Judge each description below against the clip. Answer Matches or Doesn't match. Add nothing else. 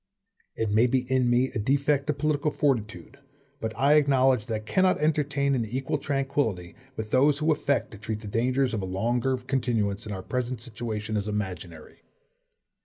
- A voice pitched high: Doesn't match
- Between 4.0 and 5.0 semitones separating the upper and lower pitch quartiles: Matches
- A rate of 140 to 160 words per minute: Doesn't match